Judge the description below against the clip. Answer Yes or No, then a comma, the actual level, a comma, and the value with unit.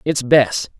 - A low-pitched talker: Yes, low, 130 Hz